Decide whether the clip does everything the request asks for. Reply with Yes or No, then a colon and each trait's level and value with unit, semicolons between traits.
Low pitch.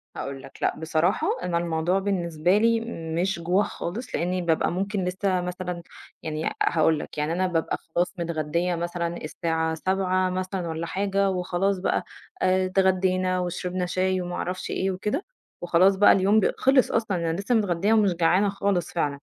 No: medium, 180 Hz